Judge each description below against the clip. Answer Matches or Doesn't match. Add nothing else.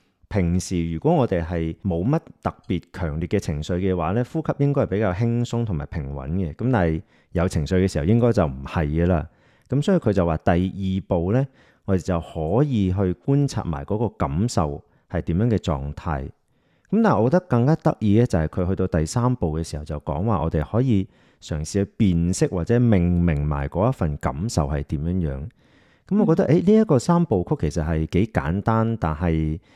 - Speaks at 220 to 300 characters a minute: Matches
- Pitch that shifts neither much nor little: Doesn't match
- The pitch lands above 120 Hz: Doesn't match